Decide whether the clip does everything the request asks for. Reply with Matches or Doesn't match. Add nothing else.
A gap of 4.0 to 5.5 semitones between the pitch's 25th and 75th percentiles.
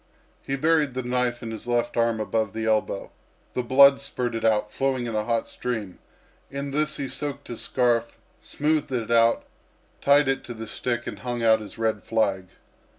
Doesn't match